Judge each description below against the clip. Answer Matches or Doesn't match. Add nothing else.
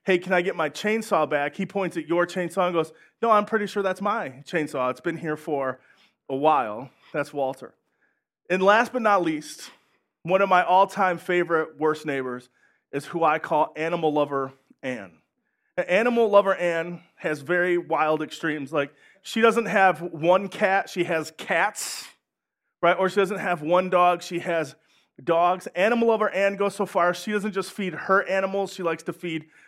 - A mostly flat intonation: Doesn't match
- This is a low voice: Doesn't match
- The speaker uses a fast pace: Doesn't match